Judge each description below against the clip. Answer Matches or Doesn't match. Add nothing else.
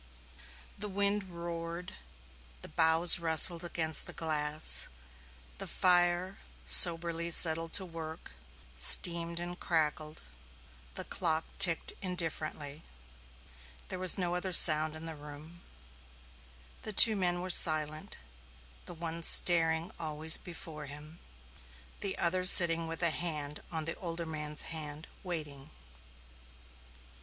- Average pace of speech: Doesn't match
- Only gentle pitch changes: Matches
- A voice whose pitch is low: Doesn't match